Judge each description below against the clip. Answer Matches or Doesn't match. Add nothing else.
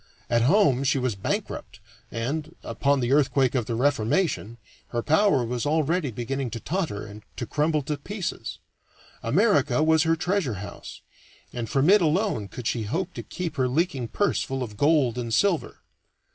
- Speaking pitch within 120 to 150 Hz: Matches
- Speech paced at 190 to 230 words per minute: Doesn't match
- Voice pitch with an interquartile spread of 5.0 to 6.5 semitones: Matches